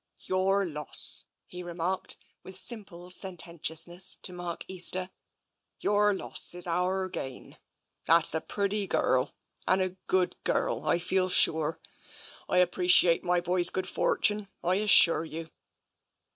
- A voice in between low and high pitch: Yes, medium, 180 Hz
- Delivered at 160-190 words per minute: No, average, 145 wpm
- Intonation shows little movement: Yes, narrow, 1.8 semitones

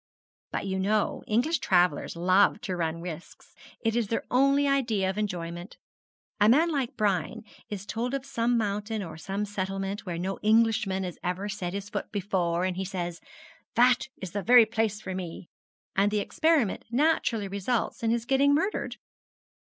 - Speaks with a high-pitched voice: Yes, high, 205 Hz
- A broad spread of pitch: No, average, 4.0 semitones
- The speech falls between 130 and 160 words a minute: No, average, 170 wpm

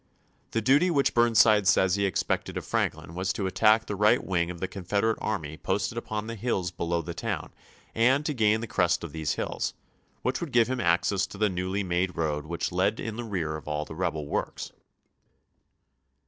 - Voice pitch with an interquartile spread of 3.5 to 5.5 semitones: Yes, average, 4.6 semitones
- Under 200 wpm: No, fast, 205 wpm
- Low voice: Yes, very low, 95 Hz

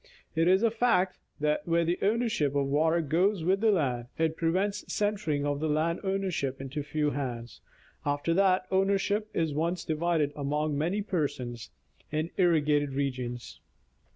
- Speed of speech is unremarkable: Yes, average, 150 wpm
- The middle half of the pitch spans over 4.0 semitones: Yes, average, 4.6 semitones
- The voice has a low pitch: No, medium, 160 Hz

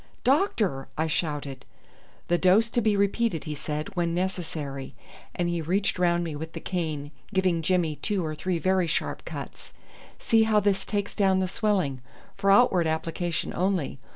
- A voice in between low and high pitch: Yes, medium, 180 Hz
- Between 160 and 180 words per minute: Yes, average, 165 wpm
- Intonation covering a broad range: No, average, 3.7 semitones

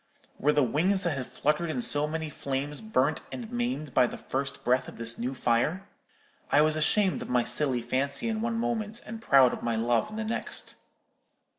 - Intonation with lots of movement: Yes, wide, 8.6 semitones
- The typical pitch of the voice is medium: Yes, medium, 150 Hz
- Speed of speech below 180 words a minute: No, average, 200 wpm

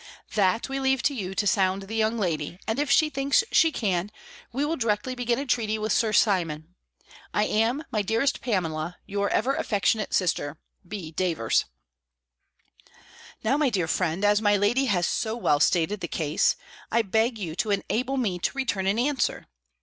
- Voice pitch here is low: No, high, 210 Hz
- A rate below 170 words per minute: No, average, 175 wpm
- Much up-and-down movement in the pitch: No, average, 4.7 semitones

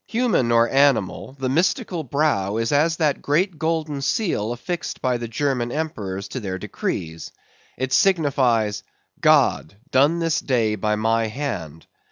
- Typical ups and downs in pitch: No, wide, 6.1 semitones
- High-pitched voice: No, low, 130 Hz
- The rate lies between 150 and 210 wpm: No, average, 140 wpm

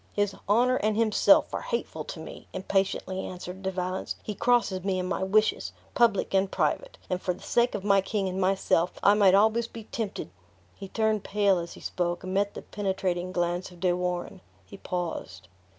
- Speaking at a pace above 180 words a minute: Yes, average, 200 wpm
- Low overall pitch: No, high, 190 Hz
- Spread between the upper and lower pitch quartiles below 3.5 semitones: Yes, narrow, 2.4 semitones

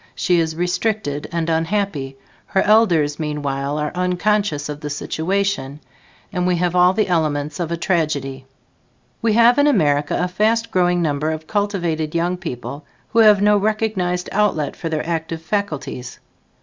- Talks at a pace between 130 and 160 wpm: Yes, average, 155 wpm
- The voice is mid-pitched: Yes, medium, 170 Hz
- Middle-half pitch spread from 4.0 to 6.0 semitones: Yes, average, 4.9 semitones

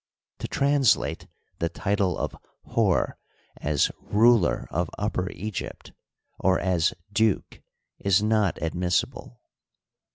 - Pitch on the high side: No, very low, 95 Hz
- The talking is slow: Yes, slow, 100 wpm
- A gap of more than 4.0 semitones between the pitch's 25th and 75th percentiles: No, average, 3.7 semitones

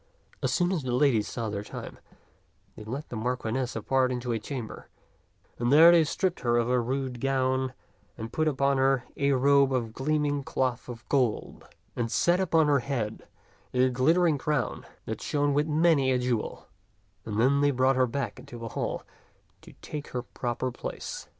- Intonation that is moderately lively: Yes, average, 3.0 semitones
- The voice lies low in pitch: Yes, low, 130 Hz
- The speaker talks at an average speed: Yes, average, 180 wpm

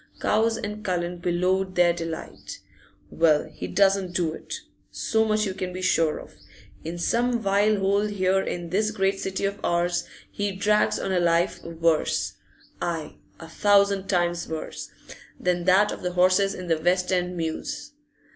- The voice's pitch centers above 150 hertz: Yes, medium, 185 Hz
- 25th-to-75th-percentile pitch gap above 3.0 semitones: No, narrow, 2.6 semitones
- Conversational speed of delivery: Yes, average, 165 wpm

